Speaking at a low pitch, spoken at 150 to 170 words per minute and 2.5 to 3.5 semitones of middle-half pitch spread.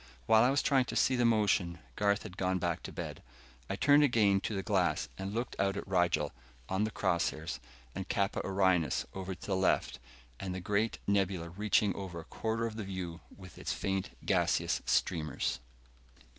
No: very low, 95 Hz; average, 190 wpm; average, 2.9 semitones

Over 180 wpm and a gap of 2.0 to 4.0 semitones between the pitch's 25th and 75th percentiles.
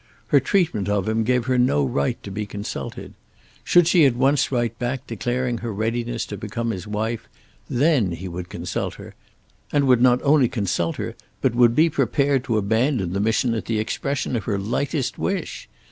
Yes: average, 190 wpm; average, 3.7 semitones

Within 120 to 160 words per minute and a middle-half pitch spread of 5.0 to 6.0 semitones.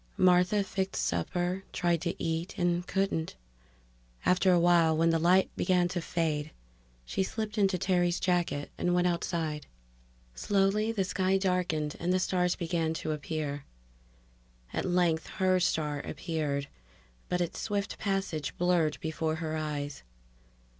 No: average, 140 wpm; narrow, 2.6 semitones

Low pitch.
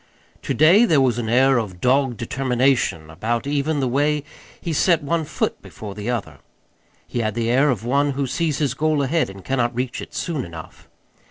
Yes: low, 130 Hz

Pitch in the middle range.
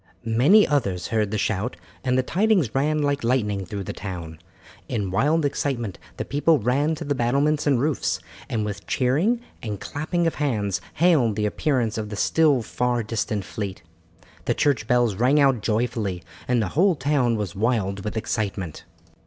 No: low, 120 Hz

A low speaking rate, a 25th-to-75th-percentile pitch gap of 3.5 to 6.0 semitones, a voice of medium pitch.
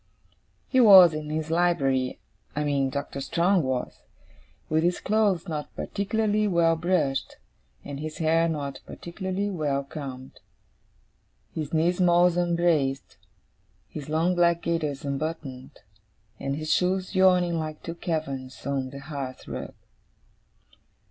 Yes: slow, 125 wpm; average, 4.0 semitones; medium, 160 Hz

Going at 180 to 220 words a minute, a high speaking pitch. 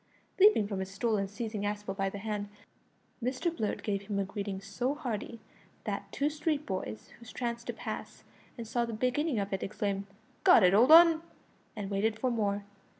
Yes: average, 190 wpm; high, 215 Hz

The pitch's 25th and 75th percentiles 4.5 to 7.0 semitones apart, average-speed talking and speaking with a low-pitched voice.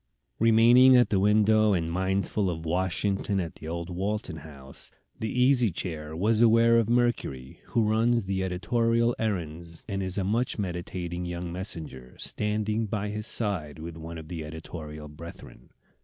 Yes: average, 4.9 semitones; average, 155 wpm; very low, 95 Hz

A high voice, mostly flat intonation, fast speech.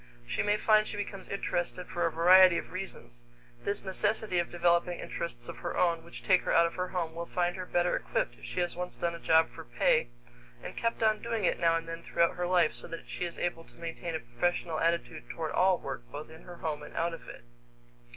No: medium, 175 Hz; narrow, 1.8 semitones; fast, 240 wpm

